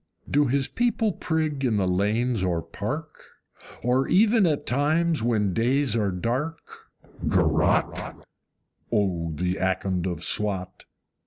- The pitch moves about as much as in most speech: No, wide, 7.6 semitones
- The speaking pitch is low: Yes, low, 120 Hz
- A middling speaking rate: No, slow, 120 wpm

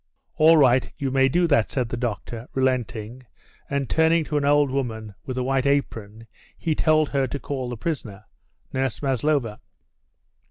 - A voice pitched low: Yes, low, 130 Hz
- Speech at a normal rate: Yes, average, 165 wpm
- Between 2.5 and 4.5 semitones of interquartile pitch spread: Yes, average, 3.2 semitones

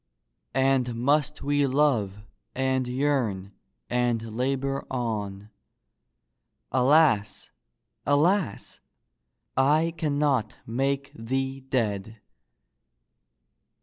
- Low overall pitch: Yes, low, 130 Hz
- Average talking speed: No, slow, 70 wpm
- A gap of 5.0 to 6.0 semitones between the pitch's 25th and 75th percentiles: No, average, 3.8 semitones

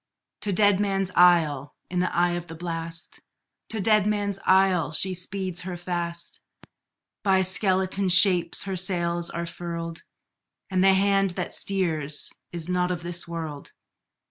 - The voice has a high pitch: No, medium, 180 Hz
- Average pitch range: No, narrow, 2.1 semitones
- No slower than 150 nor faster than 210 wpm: No, average, 140 wpm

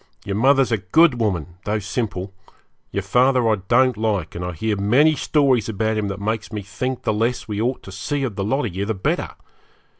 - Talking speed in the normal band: No, fast, 215 wpm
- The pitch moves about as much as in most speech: Yes, average, 4.0 semitones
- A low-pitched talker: Yes, low, 110 Hz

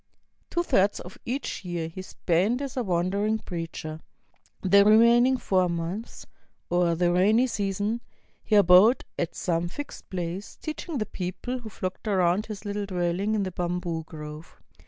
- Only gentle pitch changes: No, average, 3.8 semitones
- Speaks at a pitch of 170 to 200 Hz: Yes, high, 190 Hz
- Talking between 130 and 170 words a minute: Yes, average, 155 wpm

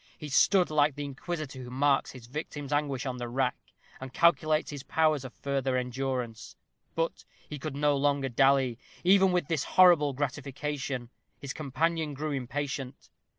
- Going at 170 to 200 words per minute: No, average, 155 wpm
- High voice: No, medium, 140 Hz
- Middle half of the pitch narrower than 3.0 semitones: Yes, narrow, 2.5 semitones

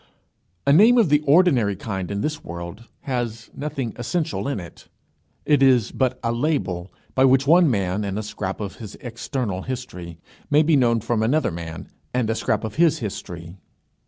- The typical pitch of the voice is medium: No, low, 115 Hz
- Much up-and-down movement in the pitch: Yes, wide, 6.1 semitones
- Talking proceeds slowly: No, average, 180 wpm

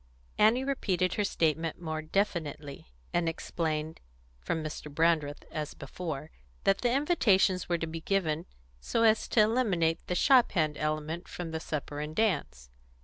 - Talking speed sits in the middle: Yes, average, 150 wpm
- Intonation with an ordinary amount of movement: Yes, average, 4.2 semitones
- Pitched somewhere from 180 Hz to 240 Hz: No, medium, 165 Hz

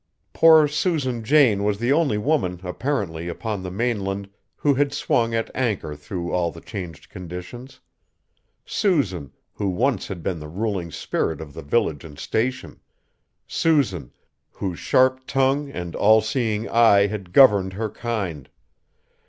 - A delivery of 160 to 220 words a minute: No, average, 145 wpm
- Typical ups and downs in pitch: No, wide, 6.4 semitones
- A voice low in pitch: Yes, low, 105 Hz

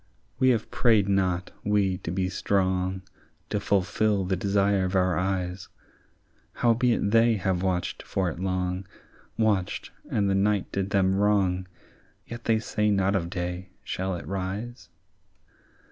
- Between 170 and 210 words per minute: No, average, 145 wpm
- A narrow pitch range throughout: Yes, narrow, 1.9 semitones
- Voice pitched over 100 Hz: No, very low, 95 Hz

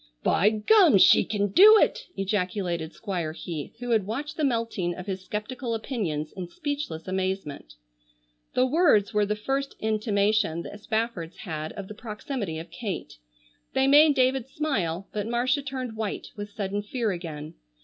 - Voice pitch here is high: Yes, high, 210 Hz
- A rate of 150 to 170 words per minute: Yes, average, 160 wpm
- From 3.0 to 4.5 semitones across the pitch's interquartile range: No, wide, 5.4 semitones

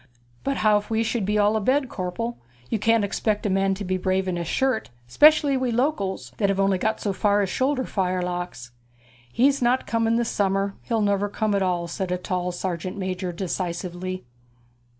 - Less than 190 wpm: No, average, 195 wpm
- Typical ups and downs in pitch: Yes, average, 3.6 semitones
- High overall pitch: Yes, high, 200 Hz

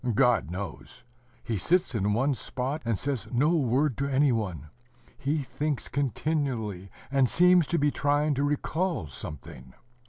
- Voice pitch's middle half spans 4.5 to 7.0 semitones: Yes, average, 5.1 semitones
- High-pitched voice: No, low, 135 Hz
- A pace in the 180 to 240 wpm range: No, average, 150 wpm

